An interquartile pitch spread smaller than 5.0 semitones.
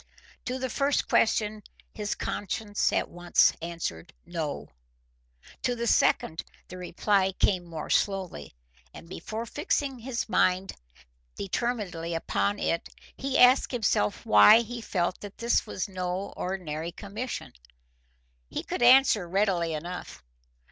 No: average, 5.3 semitones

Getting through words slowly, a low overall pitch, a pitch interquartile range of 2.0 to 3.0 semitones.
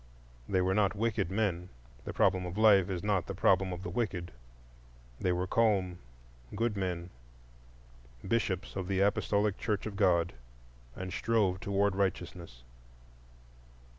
Yes: slow, 130 wpm; very low, 95 Hz; average, 2.7 semitones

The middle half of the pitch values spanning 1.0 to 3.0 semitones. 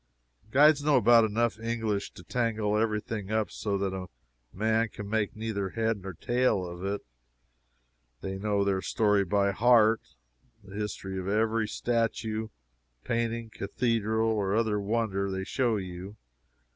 Yes: narrow, 2.4 semitones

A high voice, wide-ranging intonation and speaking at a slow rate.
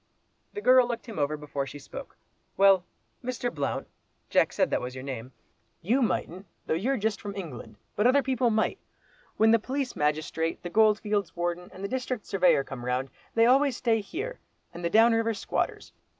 No: high, 205 Hz; wide, 7.2 semitones; average, 185 wpm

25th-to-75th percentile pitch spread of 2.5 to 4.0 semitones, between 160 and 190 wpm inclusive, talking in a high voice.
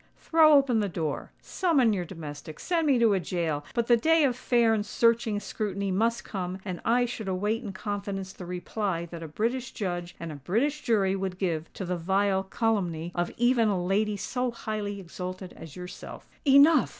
No: average, 4.5 semitones; average, 175 wpm; high, 200 Hz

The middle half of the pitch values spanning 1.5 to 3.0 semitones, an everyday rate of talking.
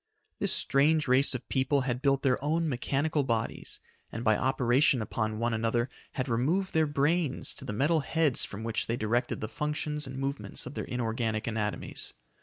No: average, 4.2 semitones; average, 180 wpm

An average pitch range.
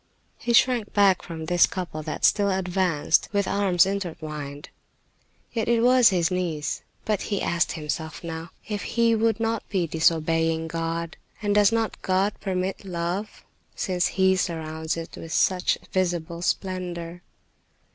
Yes: average, 3.6 semitones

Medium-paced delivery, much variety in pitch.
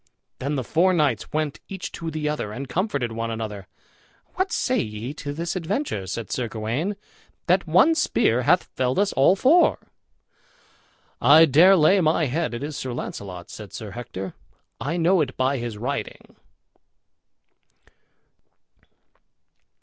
Yes: average, 145 wpm; wide, 6.7 semitones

